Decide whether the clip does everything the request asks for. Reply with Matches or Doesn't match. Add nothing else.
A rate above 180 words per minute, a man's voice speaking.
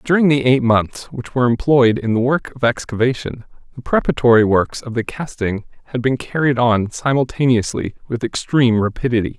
Doesn't match